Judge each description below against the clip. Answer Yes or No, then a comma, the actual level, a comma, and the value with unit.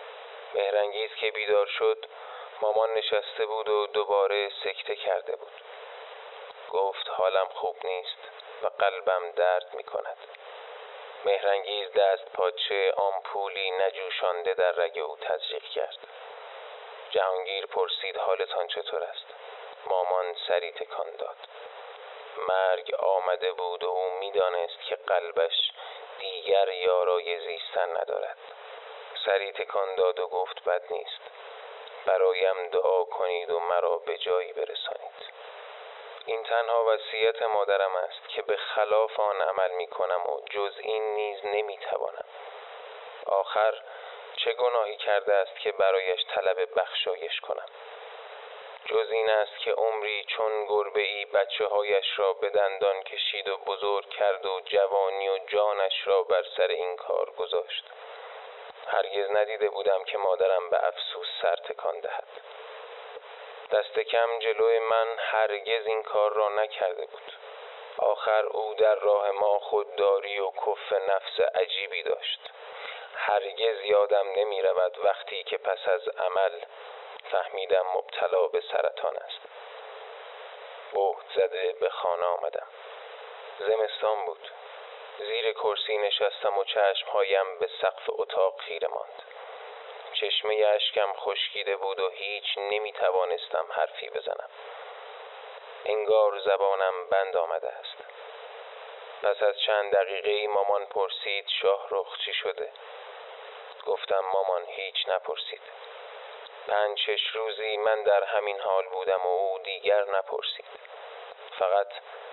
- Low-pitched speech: Yes, low, 125 Hz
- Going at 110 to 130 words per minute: Yes, average, 120 wpm